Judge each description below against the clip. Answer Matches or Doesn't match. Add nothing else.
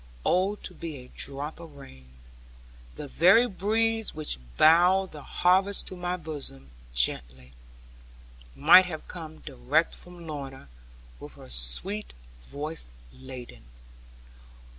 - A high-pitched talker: Doesn't match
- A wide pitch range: Matches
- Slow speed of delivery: Matches